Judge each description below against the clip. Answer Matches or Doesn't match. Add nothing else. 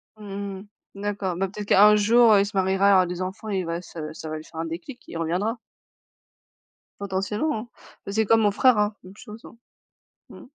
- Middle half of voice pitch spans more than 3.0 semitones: Doesn't match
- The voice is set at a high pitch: Matches